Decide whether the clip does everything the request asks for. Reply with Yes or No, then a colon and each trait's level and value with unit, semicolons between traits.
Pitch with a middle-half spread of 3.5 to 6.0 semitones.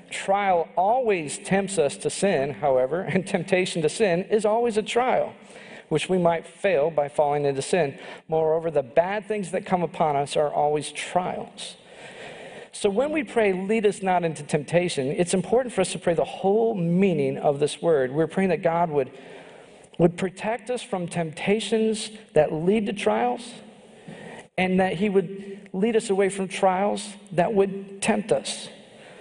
Yes: average, 4.3 semitones